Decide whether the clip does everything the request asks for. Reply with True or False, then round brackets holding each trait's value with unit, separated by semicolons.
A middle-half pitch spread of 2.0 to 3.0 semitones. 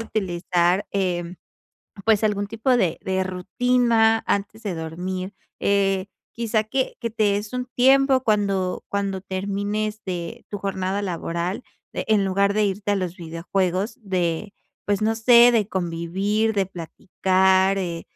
True (2.7 semitones)